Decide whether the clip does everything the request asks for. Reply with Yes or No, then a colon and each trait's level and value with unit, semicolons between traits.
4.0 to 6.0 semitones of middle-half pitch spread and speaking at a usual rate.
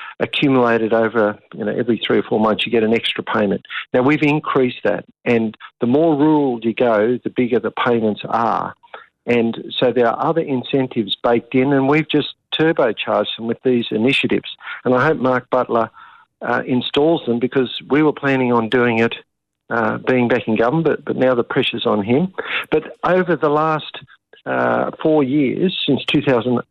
Yes: average, 4.3 semitones; average, 180 wpm